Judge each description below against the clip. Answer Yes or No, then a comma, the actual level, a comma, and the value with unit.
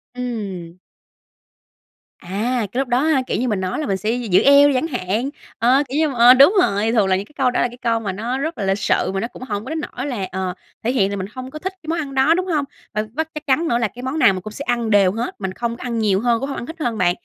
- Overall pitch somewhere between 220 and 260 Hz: Yes, high, 240 Hz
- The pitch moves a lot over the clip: No, average, 5.0 semitones